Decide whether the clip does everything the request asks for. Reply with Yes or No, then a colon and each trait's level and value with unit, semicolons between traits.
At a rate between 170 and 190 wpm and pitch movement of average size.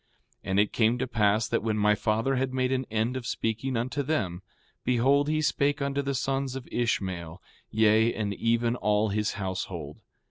Yes: average, 185 wpm; average, 3.9 semitones